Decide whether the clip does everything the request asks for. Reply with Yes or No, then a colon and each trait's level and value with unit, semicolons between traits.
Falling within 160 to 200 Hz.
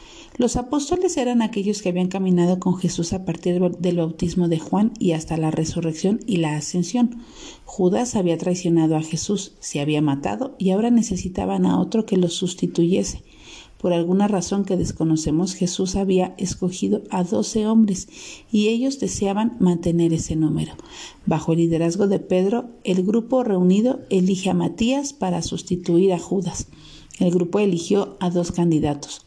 Yes: medium, 185 Hz